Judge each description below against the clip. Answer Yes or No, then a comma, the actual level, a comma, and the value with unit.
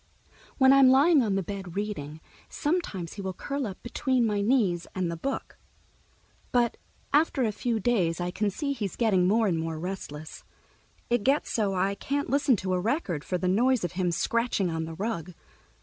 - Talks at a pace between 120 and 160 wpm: No, average, 190 wpm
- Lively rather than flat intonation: Yes, wide, 5.8 semitones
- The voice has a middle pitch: No, high, 205 Hz